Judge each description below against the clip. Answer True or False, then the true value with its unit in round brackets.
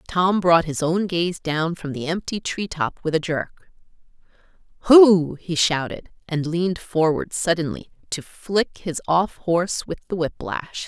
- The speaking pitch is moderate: True (170 Hz)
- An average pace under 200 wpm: True (160 wpm)